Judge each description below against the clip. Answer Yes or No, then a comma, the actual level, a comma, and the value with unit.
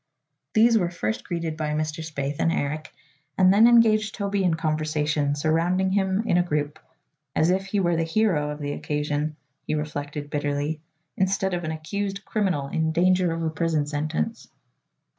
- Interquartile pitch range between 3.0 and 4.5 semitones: Yes, average, 4.0 semitones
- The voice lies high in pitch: No, medium, 160 Hz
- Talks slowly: No, average, 170 wpm